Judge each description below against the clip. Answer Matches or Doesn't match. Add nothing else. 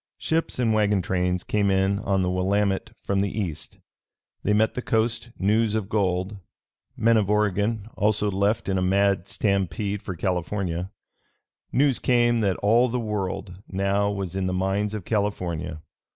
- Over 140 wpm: Matches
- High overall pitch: Doesn't match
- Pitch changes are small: Matches